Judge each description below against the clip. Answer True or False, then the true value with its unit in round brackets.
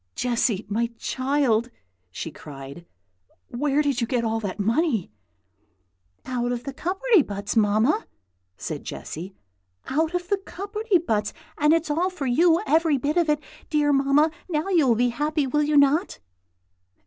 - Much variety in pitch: True (5.7 semitones)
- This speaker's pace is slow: False (155 wpm)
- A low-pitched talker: False (280 Hz)